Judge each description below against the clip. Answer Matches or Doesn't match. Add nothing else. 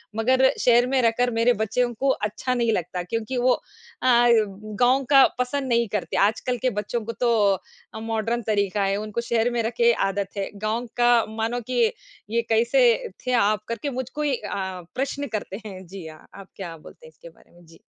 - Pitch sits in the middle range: Doesn't match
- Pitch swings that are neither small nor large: Matches